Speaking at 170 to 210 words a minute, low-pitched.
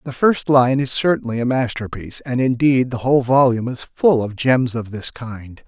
Yes: average, 200 wpm; low, 125 Hz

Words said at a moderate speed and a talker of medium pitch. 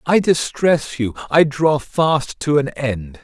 Yes: average, 165 wpm; medium, 145 Hz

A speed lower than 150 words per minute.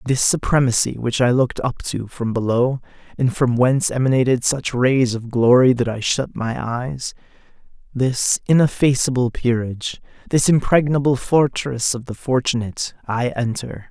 Yes: average, 140 wpm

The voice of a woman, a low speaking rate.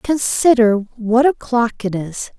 Yes: female; slow, 125 wpm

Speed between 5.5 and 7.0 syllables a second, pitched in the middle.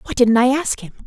No: 5.8 syllables/s; high, 245 Hz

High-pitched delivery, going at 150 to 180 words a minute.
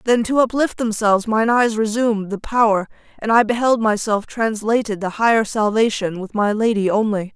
Yes: high, 220 Hz; average, 170 wpm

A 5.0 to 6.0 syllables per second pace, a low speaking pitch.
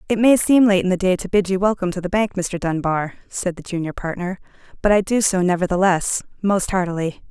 No: 5.9 syllables/s; high, 190 Hz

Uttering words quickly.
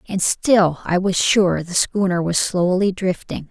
No: average, 170 wpm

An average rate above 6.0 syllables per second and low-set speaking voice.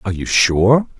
No: 4.9 syllables/s; low, 110 Hz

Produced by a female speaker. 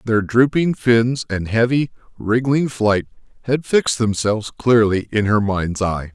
No: male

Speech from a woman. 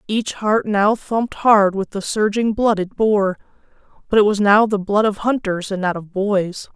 Yes: female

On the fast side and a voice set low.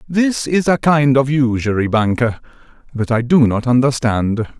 No: average, 155 wpm; low, 130 Hz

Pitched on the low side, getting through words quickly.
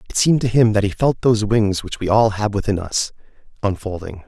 Yes: low, 105 Hz; fast, 225 wpm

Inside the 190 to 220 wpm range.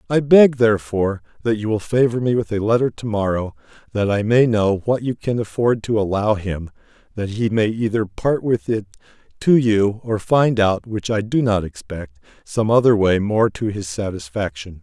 Yes: average, 195 wpm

